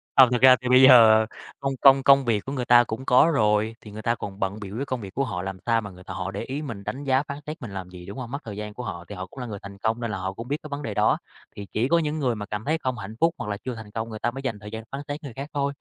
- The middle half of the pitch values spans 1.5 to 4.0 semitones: No, average, 4.6 semitones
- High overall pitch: No, low, 115 Hz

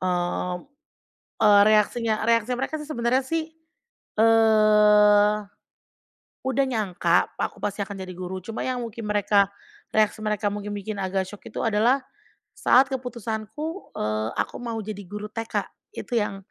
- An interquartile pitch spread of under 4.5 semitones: Yes, narrow, 2.6 semitones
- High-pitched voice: Yes, high, 215 Hz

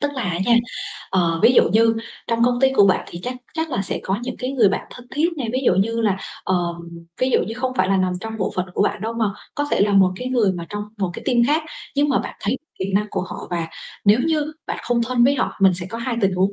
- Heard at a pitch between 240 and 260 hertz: No, high, 225 Hz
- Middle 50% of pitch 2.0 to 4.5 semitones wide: No, average, 4.9 semitones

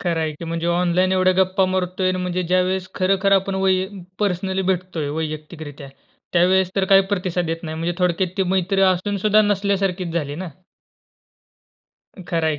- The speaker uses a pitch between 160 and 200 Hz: Yes, medium, 185 Hz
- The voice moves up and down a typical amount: No, narrow, 1.9 semitones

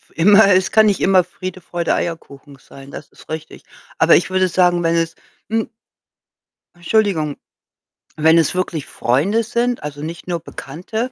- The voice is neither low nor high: Yes, medium, 175 Hz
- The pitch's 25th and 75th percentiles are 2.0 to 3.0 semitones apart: No, average, 3.7 semitones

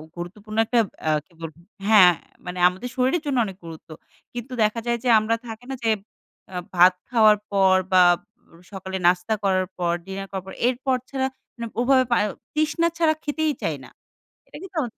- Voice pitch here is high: Yes, high, 215 Hz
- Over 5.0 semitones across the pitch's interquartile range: Yes, wide, 5.4 semitones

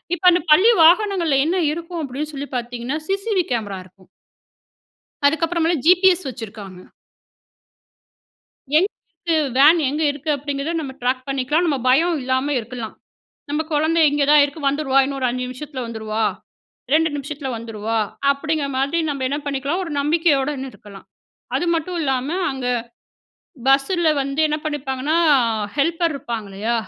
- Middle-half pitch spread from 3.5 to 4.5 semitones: Yes, average, 4.0 semitones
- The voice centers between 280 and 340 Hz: Yes, very high, 285 Hz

